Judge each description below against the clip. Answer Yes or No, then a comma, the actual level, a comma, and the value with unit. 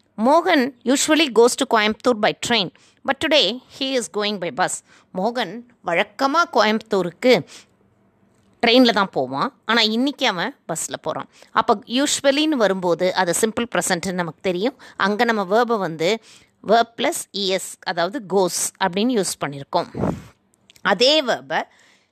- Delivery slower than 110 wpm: No, fast, 130 wpm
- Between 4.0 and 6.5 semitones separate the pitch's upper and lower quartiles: Yes, average, 5.1 semitones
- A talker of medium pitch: No, high, 225 Hz